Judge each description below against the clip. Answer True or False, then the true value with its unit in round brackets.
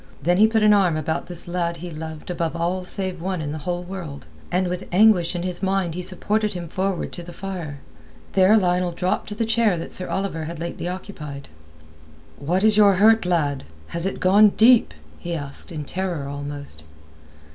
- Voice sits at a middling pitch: True (180 Hz)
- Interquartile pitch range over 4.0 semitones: False (2.9 semitones)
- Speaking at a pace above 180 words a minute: True (195 wpm)